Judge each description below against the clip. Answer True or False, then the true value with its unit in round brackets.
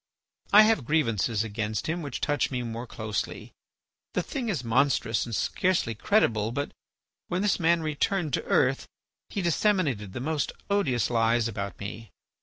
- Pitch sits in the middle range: False (130 Hz)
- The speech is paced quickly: False (155 wpm)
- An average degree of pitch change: False (7.1 semitones)